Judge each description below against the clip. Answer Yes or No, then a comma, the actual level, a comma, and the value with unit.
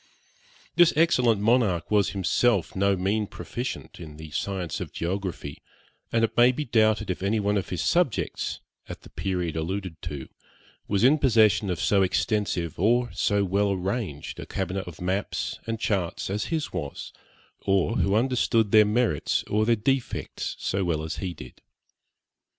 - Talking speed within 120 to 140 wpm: No, average, 160 wpm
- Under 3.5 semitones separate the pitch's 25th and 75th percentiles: No, average, 3.8 semitones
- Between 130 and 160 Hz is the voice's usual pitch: No, low, 100 Hz